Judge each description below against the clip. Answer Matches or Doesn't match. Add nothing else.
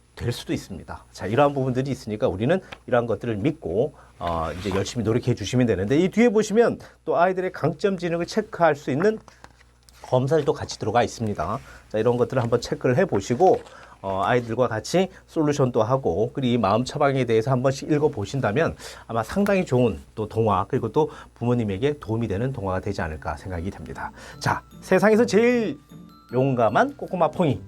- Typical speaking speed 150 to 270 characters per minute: Doesn't match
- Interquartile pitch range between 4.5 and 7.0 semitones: Doesn't match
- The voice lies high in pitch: Doesn't match